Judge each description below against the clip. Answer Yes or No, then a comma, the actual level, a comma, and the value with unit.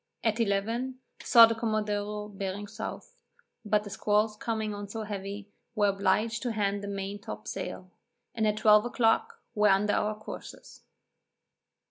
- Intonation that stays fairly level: Yes, narrow, 1.6 semitones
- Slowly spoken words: No, average, 150 wpm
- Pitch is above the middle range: Yes, high, 210 Hz